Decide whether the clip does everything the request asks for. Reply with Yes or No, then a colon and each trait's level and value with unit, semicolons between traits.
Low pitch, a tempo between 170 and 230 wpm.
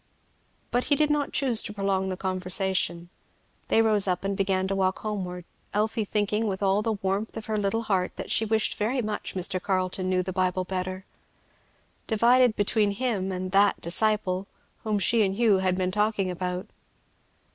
No: high, 195 Hz; average, 180 wpm